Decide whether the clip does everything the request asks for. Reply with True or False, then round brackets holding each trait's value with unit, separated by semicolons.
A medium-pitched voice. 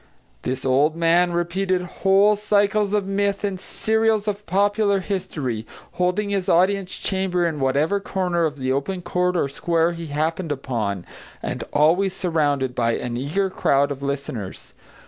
True (175 Hz)